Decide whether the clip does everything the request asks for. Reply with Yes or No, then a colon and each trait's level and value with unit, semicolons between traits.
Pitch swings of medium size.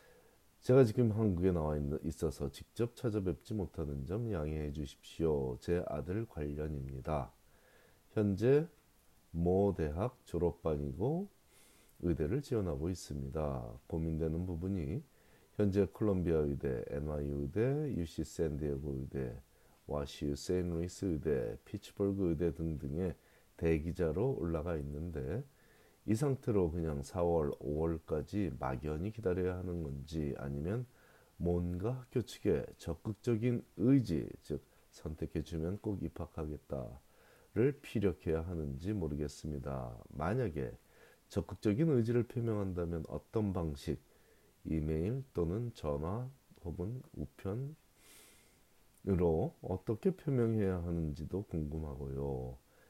No: wide, 5.9 semitones